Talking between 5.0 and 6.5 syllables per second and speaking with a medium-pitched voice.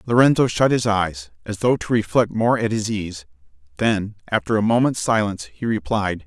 No: 5.1 syllables/s; low, 105 Hz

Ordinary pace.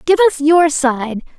Yes: average, 175 wpm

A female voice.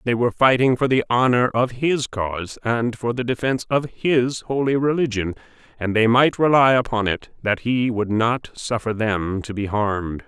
No: male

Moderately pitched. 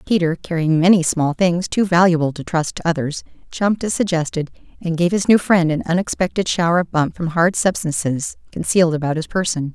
Yes: medium, 170 Hz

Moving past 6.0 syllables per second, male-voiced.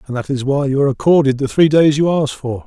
Yes: 6.3 syllables/s; male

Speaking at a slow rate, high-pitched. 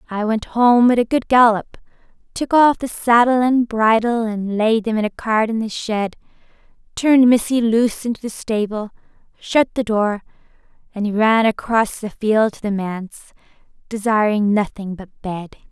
No: average, 165 wpm; high, 220 Hz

